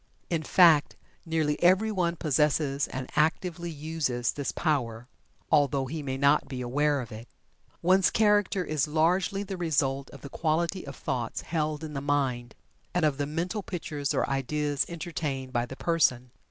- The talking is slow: No, average, 160 wpm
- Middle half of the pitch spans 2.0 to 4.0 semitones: Yes, average, 3.7 semitones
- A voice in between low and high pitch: Yes, medium, 150 Hz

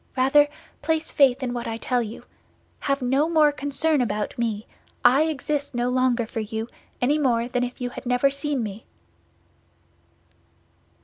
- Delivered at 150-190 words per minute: Yes, average, 160 wpm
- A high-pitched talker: Yes, very high, 255 Hz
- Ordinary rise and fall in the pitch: Yes, average, 3.2 semitones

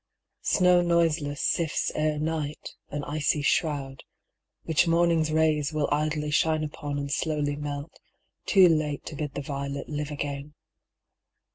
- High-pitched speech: No, medium, 150 Hz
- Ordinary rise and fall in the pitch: No, narrow, 1.7 semitones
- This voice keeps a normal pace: No, slow, 130 wpm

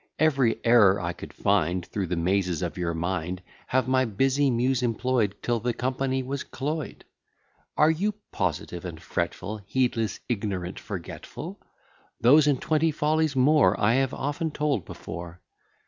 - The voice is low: Yes, low, 115 Hz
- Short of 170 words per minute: Yes, average, 145 wpm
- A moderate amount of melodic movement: No, wide, 6.6 semitones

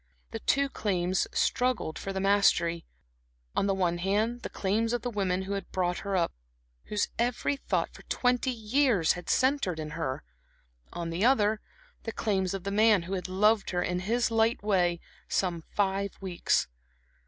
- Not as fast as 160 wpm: No, average, 175 wpm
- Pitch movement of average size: Yes, average, 3.9 semitones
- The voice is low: No, high, 200 Hz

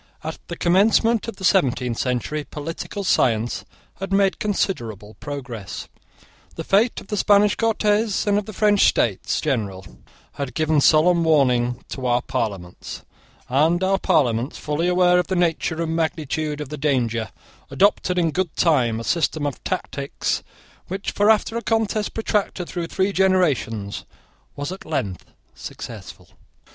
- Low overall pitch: No, medium, 160 Hz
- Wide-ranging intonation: Yes, wide, 7.1 semitones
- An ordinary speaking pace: Yes, average, 145 wpm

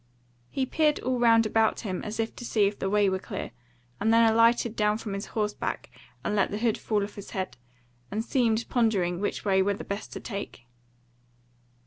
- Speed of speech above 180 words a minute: Yes, average, 195 wpm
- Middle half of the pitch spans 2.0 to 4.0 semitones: Yes, narrow, 2.4 semitones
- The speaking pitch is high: Yes, high, 215 Hz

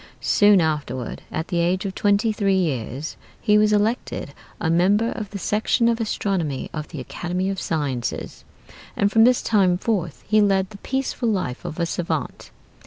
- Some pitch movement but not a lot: Yes, average, 4.6 semitones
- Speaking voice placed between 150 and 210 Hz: Yes, high, 190 Hz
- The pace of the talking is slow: No, average, 175 wpm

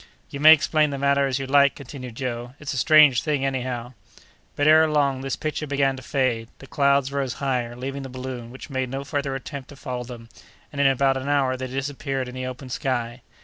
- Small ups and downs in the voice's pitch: Yes, narrow, 1.6 semitones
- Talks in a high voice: No, low, 135 Hz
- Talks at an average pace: No, fast, 225 wpm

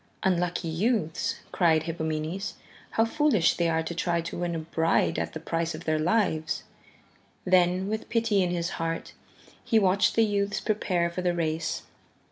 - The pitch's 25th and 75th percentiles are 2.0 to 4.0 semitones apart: Yes, average, 3.5 semitones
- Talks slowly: No, average, 165 wpm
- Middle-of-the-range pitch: Yes, medium, 175 Hz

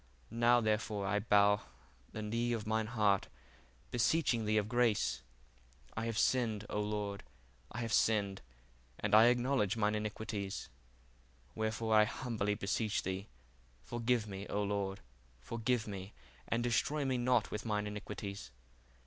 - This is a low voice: Yes, low, 110 Hz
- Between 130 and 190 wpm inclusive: Yes, average, 140 wpm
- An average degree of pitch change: No, narrow, 2.3 semitones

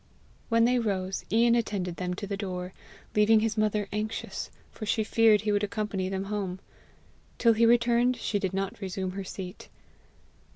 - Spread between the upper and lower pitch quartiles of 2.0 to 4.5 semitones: Yes, average, 2.9 semitones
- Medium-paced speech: Yes, average, 170 wpm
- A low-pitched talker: No, high, 210 Hz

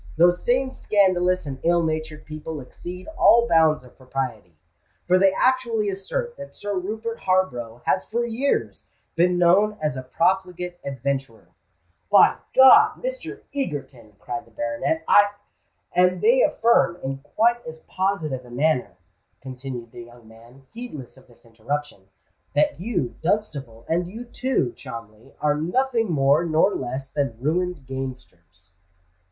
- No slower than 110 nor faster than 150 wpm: Yes, average, 140 wpm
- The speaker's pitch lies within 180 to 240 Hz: No, medium, 160 Hz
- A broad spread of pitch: Yes, wide, 7.6 semitones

